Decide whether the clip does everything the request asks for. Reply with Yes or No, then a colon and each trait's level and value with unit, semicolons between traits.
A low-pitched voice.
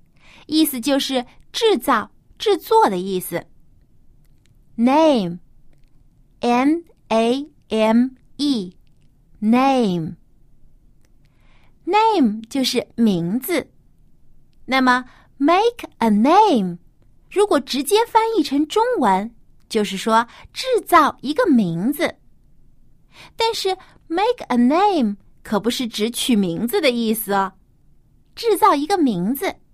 No: very high, 255 Hz